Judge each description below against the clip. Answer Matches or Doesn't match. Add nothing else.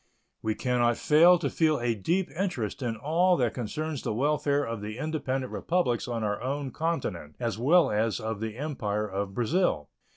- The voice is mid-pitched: Doesn't match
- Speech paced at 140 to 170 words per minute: Doesn't match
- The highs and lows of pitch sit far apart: Matches